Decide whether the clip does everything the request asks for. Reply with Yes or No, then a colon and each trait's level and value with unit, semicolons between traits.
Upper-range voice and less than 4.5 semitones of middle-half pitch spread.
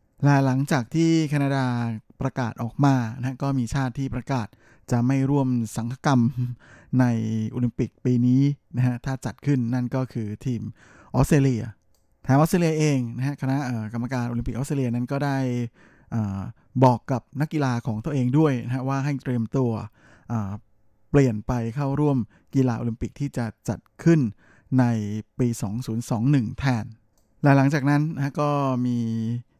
No: low, 125 Hz; average, 2.8 semitones